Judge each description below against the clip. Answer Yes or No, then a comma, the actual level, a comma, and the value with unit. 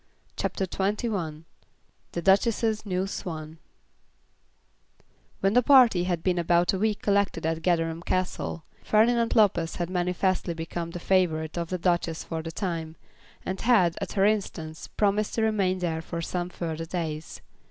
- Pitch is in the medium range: Yes, medium, 180 Hz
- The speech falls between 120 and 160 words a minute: Yes, average, 150 wpm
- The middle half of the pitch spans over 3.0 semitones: Yes, average, 3.4 semitones